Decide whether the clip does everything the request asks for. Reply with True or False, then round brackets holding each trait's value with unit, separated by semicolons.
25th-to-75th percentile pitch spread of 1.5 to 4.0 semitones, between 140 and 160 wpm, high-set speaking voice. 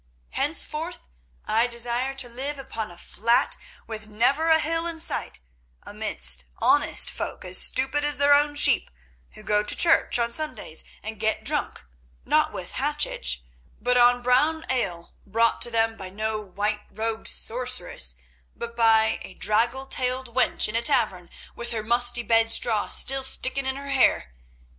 True (3.6 semitones; 155 wpm; 235 Hz)